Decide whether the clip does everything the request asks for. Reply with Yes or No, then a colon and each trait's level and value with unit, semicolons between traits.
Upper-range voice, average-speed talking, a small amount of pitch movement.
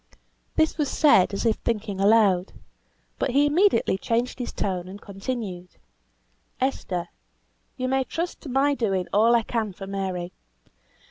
No: high, 220 Hz; average, 145 wpm; average, 5.2 semitones